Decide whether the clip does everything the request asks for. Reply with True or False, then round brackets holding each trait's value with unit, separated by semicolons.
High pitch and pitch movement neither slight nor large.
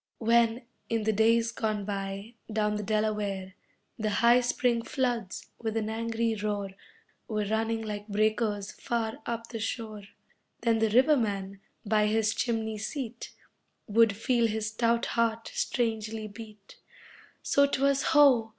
False (220 Hz; 1.6 semitones)